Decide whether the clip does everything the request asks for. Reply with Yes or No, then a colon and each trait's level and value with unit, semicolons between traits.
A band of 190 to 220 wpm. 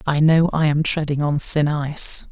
Yes: fast, 205 wpm